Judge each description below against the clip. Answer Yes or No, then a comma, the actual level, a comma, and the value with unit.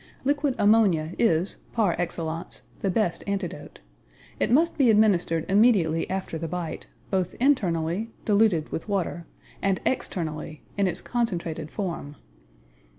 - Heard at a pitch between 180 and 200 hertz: Yes, medium, 185 Hz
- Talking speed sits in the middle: No, slow, 125 wpm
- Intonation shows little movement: No, average, 4.8 semitones